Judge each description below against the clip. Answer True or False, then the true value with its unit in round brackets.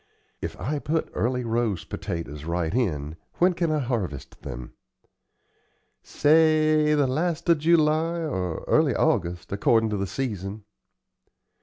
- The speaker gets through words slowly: True (130 wpm)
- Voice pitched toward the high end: False (120 Hz)